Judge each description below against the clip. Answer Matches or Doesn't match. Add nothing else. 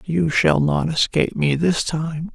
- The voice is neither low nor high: Matches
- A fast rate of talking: Doesn't match